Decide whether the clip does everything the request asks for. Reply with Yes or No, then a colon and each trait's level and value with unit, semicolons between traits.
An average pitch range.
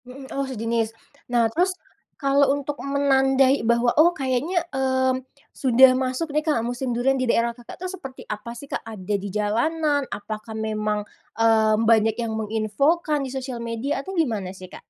Yes: average, 3.7 semitones